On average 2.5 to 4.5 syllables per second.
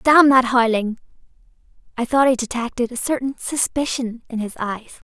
No: 5.0 syllables/s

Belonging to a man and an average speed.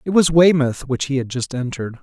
No: male; fast, 235 wpm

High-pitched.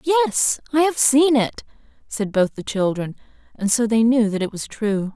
Yes: high, 235 Hz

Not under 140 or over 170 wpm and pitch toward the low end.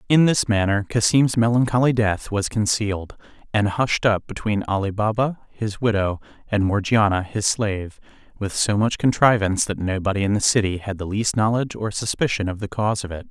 No: average, 180 wpm; low, 105 Hz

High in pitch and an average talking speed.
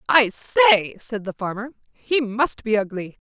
Yes: high, 235 Hz; average, 165 wpm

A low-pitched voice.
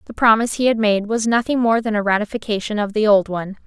No: high, 215 Hz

